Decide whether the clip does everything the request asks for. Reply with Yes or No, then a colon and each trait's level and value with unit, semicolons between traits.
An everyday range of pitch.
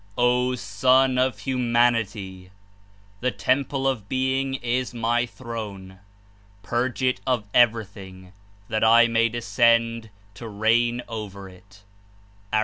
Yes: average, 3.3 semitones